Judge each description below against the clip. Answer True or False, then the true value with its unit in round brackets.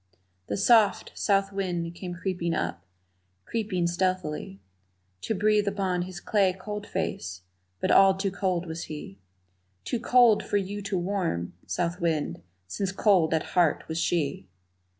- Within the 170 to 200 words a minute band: False (145 wpm)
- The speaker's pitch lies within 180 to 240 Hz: True (185 Hz)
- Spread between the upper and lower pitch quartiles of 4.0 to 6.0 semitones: False (3.0 semitones)